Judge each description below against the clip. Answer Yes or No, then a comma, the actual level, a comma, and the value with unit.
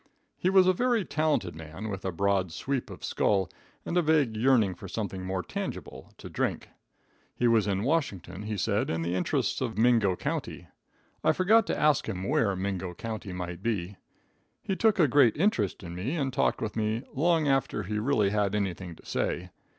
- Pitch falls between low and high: No, low, 105 Hz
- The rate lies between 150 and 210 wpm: Yes, average, 190 wpm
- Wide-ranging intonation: Yes, wide, 6.9 semitones